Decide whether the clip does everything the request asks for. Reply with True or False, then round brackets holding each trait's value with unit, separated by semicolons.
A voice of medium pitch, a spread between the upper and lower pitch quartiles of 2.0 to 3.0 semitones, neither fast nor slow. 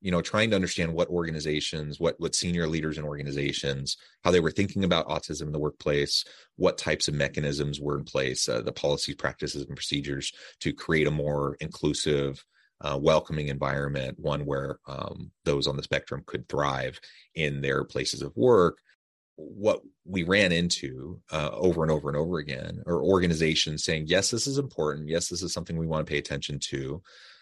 False (75 Hz; 2.7 semitones; 185 wpm)